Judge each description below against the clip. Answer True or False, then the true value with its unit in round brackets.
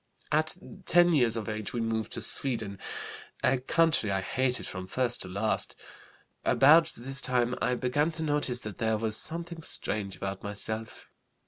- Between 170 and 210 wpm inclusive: False (160 wpm)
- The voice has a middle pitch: False (120 Hz)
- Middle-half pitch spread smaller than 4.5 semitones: False (5.2 semitones)